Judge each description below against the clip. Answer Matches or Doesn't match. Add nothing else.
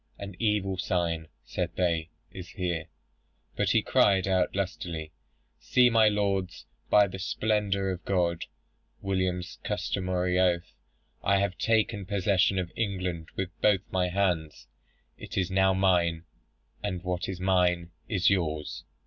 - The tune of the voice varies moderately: Doesn't match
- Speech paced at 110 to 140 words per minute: Matches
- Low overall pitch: Matches